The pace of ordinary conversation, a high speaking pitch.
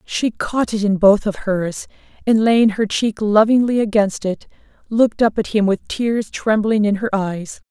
Yes: average, 185 wpm; high, 210 Hz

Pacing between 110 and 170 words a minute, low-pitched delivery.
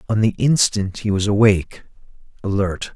Yes: average, 140 wpm; low, 105 Hz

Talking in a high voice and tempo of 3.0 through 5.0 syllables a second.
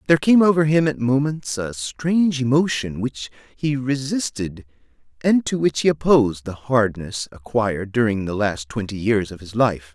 No: low, 125 Hz; 4.8 syllables/s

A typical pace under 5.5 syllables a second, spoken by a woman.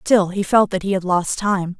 Yes: 4.7 syllables/s; female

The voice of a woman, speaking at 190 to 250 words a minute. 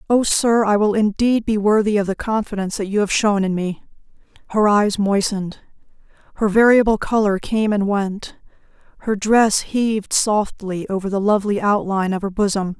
No: female; average, 170 wpm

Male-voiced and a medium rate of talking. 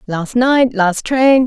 No: female; average, 165 wpm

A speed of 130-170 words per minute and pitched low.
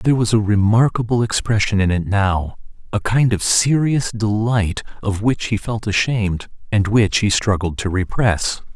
Yes: average, 165 wpm; low, 105 Hz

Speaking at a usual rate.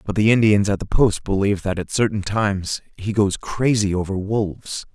Yes: average, 195 wpm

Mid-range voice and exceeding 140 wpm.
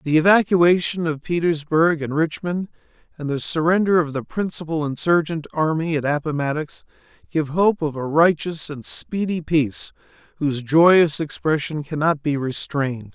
No: medium, 155 Hz; slow, 135 wpm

